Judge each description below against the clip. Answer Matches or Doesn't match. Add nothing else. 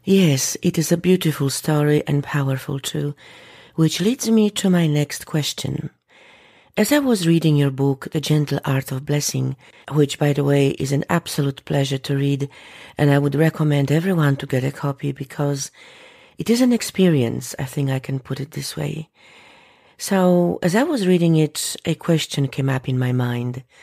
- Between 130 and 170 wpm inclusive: Doesn't match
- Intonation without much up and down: Doesn't match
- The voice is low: Doesn't match